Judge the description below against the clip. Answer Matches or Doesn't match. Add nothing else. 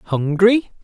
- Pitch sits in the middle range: Doesn't match